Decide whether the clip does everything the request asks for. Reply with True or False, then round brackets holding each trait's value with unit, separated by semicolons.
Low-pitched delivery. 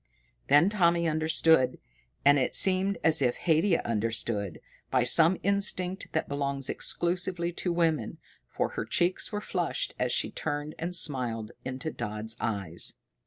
False (155 Hz)